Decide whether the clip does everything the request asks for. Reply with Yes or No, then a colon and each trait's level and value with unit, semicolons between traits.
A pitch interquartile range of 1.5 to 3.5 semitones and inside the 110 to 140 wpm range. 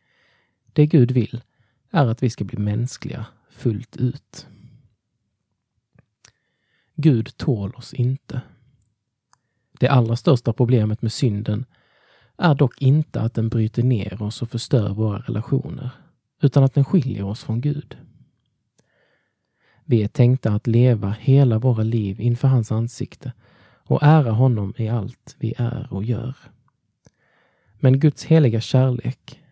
Yes: average, 3.1 semitones; average, 130 wpm